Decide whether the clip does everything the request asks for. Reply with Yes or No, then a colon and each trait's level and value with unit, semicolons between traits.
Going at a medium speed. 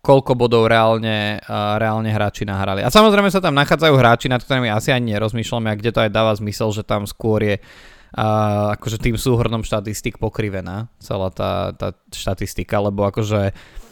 No: fast, 175 wpm